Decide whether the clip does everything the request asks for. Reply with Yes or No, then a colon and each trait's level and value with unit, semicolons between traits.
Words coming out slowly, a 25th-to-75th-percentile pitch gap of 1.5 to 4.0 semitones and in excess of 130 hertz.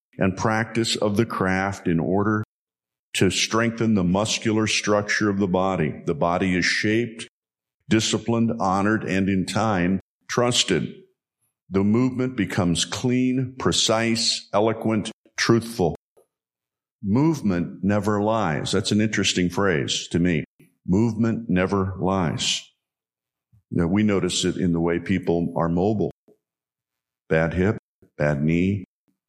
No: slow, 120 wpm; average, 3.7 semitones; low, 100 Hz